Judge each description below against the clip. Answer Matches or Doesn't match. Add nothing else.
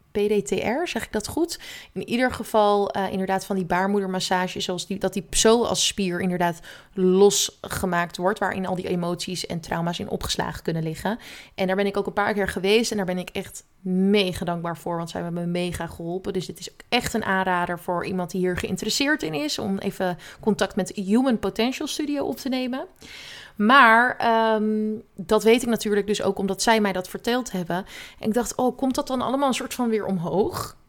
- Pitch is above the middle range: Matches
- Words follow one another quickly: Matches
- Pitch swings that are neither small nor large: Matches